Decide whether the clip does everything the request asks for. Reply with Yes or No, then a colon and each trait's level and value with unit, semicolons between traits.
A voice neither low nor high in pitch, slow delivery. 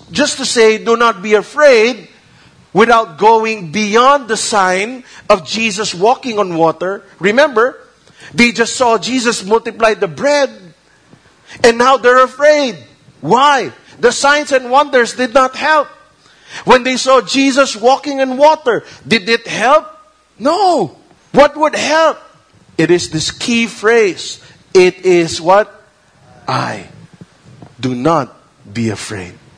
No: high, 230 Hz; slow, 130 wpm